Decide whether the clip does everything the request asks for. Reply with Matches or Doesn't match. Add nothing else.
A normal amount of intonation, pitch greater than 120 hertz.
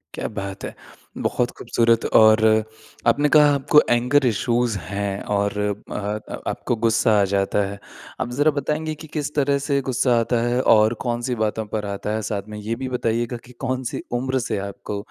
Doesn't match